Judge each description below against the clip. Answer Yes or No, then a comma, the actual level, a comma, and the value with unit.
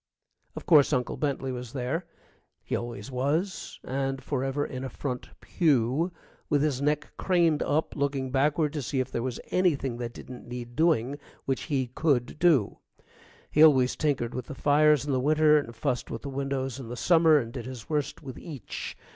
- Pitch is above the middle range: No, low, 135 Hz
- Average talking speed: Yes, average, 185 wpm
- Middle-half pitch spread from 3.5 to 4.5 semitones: No, average, 3.1 semitones